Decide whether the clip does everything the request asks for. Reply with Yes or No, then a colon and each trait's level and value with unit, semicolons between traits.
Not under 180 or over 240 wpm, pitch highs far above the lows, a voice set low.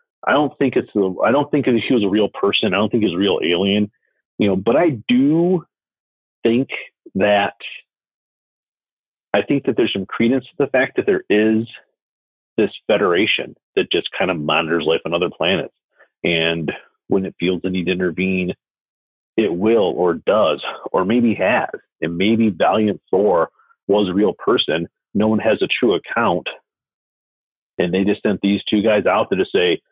Yes: average, 185 wpm; wide, 5.7 semitones; low, 110 Hz